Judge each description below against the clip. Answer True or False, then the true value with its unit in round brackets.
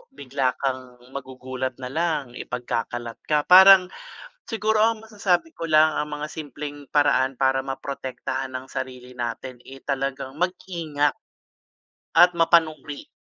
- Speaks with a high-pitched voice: False (140 Hz)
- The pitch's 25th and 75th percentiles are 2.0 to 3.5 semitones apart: False (4.2 semitones)